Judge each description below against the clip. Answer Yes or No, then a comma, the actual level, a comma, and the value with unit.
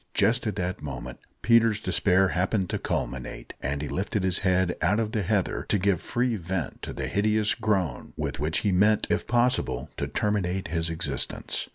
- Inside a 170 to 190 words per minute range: Yes, average, 185 wpm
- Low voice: Yes, very low, 95 Hz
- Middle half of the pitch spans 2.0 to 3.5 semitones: No, average, 3.9 semitones